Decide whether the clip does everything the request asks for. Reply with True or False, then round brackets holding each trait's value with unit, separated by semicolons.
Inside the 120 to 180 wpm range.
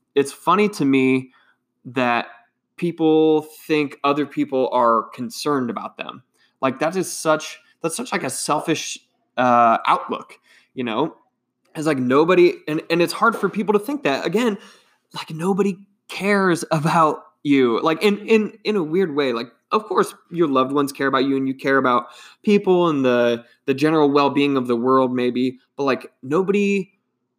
True (170 wpm)